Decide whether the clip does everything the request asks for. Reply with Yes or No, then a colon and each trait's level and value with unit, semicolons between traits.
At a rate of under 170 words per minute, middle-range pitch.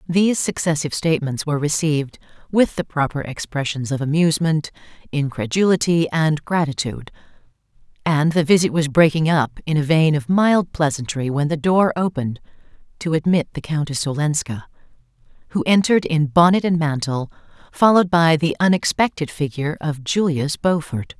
Yes: average, 140 wpm; medium, 155 Hz